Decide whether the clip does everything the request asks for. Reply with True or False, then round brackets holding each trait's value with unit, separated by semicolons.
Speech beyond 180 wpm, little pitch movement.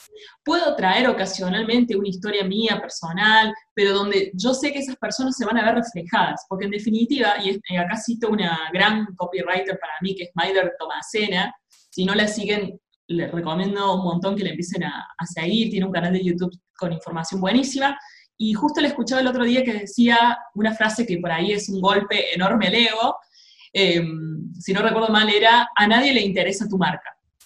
False (190 wpm; 3.6 semitones)